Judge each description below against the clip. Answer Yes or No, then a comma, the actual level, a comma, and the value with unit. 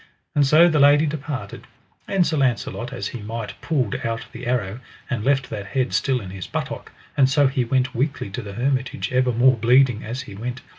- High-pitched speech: No, low, 125 Hz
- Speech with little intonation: No, average, 3.2 semitones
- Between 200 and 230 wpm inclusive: Yes, fast, 205 wpm